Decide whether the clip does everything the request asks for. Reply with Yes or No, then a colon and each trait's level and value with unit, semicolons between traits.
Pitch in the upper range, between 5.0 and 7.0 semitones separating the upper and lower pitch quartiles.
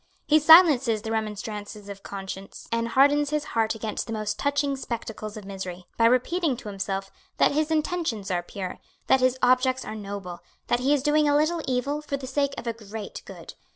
Yes: high, 235 Hz; wide, 5.5 semitones